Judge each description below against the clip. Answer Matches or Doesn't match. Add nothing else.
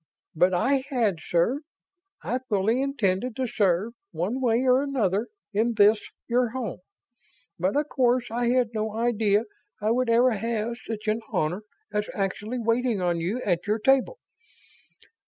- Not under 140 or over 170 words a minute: Matches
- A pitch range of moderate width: Matches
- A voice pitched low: Doesn't match